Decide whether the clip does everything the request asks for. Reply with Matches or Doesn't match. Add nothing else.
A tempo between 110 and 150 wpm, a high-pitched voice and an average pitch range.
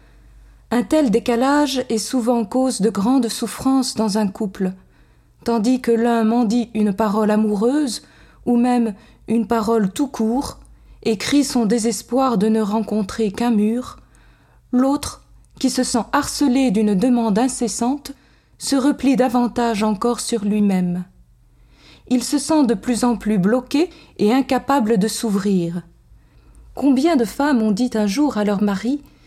Matches